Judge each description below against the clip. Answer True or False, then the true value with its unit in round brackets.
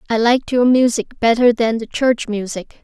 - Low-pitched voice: False (230 Hz)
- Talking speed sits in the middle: True (190 wpm)